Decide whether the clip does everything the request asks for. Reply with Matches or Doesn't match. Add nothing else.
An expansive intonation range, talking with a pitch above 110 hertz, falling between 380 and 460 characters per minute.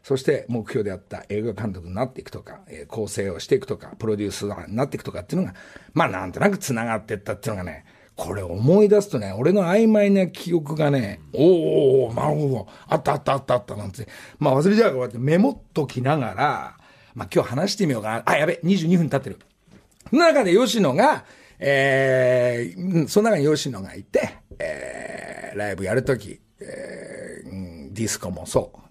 Matches